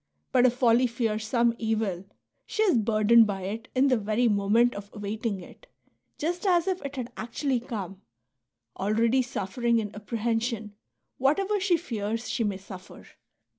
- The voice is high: Yes, high, 230 Hz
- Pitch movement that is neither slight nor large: Yes, average, 3.4 semitones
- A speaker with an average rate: Yes, average, 160 wpm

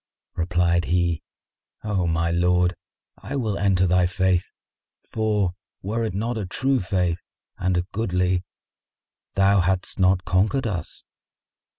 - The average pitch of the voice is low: Yes, very low, 95 Hz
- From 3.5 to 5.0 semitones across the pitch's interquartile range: No, narrow, 2.5 semitones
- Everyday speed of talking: No, slow, 125 wpm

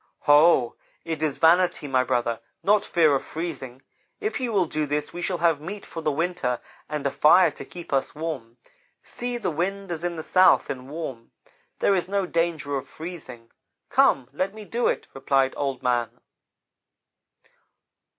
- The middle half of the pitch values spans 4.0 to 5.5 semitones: Yes, average, 4.7 semitones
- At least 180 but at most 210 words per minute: No, average, 170 wpm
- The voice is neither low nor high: Yes, medium, 160 Hz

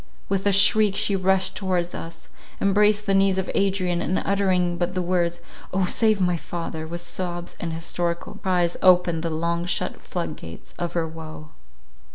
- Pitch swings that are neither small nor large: No, narrow, 2.1 semitones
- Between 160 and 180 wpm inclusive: Yes, average, 170 wpm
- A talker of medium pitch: Yes, medium, 180 Hz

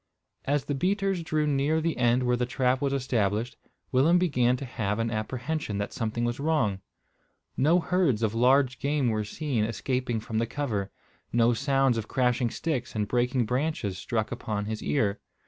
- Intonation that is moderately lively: Yes, average, 4.1 semitones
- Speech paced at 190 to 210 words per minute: No, average, 175 wpm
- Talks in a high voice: No, low, 125 Hz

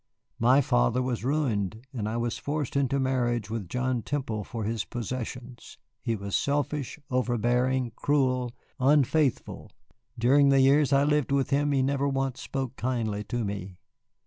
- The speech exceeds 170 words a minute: No, average, 150 wpm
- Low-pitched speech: Yes, low, 125 Hz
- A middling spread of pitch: Yes, average, 3.1 semitones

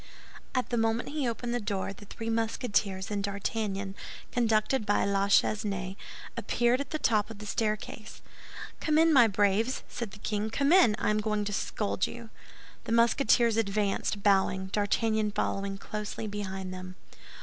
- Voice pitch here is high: Yes, high, 210 Hz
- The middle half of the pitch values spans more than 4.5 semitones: No, narrow, 2.5 semitones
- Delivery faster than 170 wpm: No, average, 160 wpm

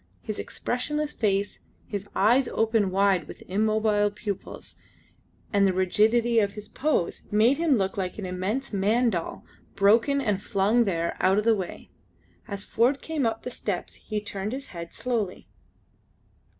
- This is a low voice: No, high, 210 Hz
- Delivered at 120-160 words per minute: Yes, average, 155 wpm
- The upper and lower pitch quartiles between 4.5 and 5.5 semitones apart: No, average, 3.3 semitones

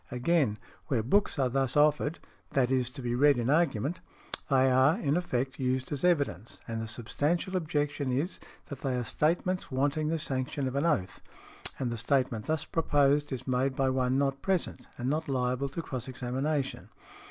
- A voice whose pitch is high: No, low, 135 Hz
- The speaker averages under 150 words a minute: No, average, 180 wpm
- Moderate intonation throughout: Yes, average, 3.0 semitones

